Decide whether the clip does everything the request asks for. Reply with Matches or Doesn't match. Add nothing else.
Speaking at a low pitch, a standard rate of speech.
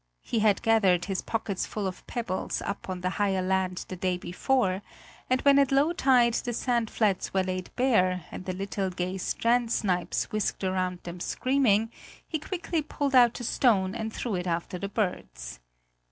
Doesn't match